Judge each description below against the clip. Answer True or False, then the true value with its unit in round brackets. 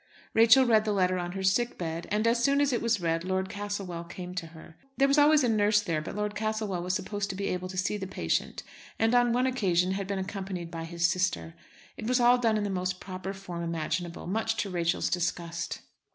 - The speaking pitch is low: False (190 Hz)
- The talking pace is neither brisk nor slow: False (230 wpm)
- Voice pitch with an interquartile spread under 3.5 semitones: False (3.8 semitones)